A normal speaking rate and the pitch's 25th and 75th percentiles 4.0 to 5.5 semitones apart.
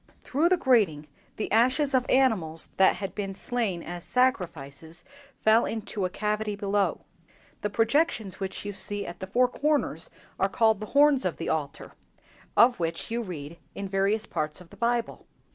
Yes: average, 170 wpm; average, 4.7 semitones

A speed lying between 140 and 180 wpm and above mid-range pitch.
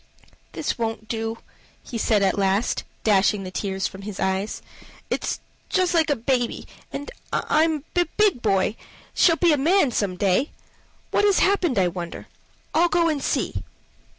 Yes: average, 160 wpm; high, 230 Hz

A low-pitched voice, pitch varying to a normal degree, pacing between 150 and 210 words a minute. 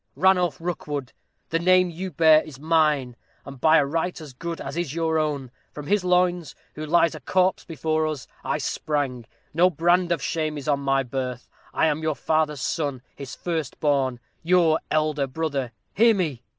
No: medium, 155 Hz; average, 3.4 semitones; average, 180 wpm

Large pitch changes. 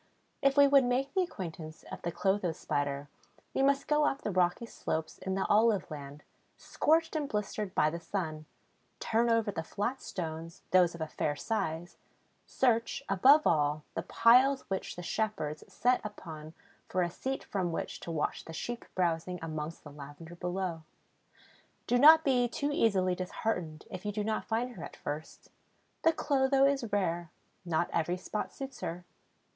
Yes: wide, 7.1 semitones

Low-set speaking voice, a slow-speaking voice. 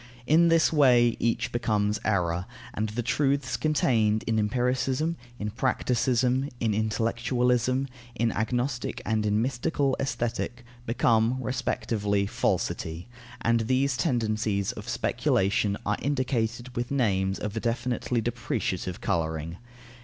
Yes: low, 115 Hz; slow, 115 wpm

